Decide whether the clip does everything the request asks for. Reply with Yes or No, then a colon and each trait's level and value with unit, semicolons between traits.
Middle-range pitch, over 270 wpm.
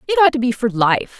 No: very high, 255 Hz; fast, 300 wpm